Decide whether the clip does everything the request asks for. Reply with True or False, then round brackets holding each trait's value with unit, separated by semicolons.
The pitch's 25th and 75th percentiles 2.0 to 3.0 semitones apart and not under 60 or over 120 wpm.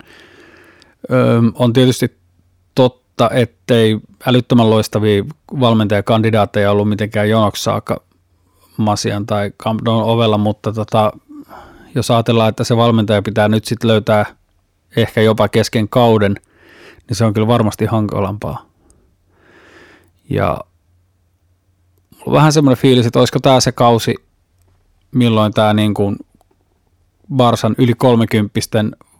True (2.7 semitones; 105 wpm)